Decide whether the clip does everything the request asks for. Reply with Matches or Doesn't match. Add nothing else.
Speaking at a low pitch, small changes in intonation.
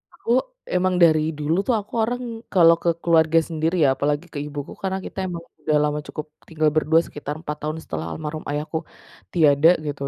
Doesn't match